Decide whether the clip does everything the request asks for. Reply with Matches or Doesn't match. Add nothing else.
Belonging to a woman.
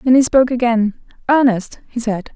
Matches